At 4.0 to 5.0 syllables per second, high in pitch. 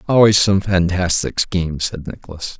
No: 4.9 syllables/s; very low, 90 Hz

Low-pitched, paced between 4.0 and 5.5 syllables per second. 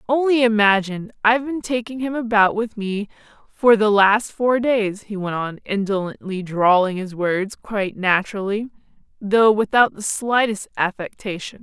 No: high, 210 Hz; 4.7 syllables/s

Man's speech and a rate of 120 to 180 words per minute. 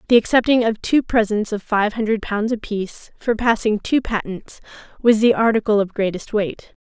No: female; average, 175 wpm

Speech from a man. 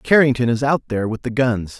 Yes: male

